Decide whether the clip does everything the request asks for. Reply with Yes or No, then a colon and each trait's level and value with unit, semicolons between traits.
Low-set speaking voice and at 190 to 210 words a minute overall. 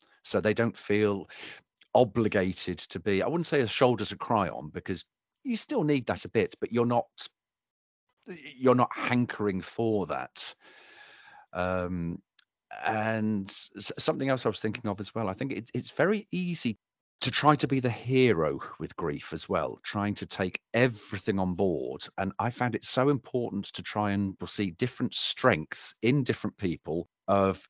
No: low, 110 Hz; average, 170 wpm